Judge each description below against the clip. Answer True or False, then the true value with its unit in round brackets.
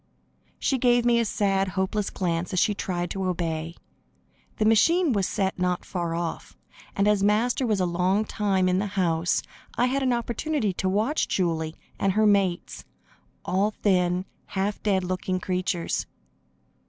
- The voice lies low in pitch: False (195 Hz)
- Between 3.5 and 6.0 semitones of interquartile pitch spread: False (3.0 semitones)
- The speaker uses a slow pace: False (160 wpm)